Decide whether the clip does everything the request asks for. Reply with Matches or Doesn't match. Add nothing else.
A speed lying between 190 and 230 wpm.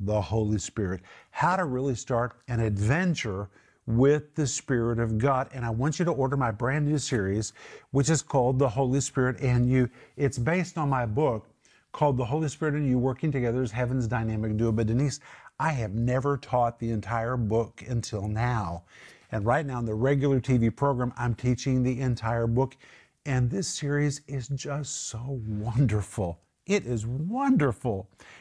Doesn't match